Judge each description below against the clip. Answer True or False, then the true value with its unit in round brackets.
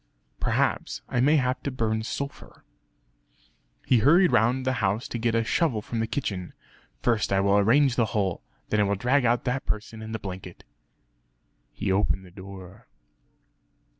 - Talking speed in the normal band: True (165 wpm)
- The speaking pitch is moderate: False (110 Hz)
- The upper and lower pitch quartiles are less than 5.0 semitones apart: True (4.2 semitones)